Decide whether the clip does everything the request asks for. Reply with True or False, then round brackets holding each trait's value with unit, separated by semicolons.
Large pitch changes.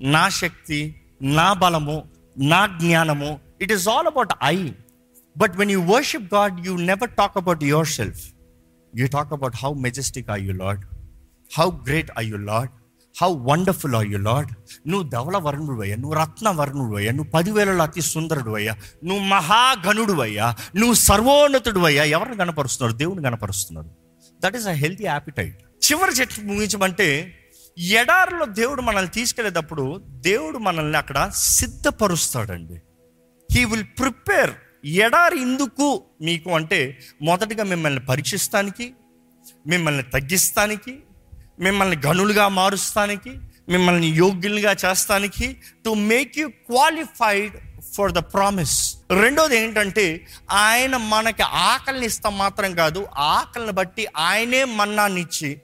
True (7.7 semitones)